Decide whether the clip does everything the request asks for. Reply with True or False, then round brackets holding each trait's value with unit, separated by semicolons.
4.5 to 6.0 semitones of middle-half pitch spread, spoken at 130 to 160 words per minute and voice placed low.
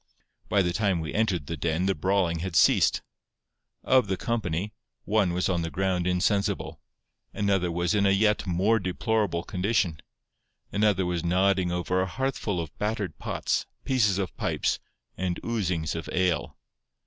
False (2.8 semitones; 155 wpm; 95 Hz)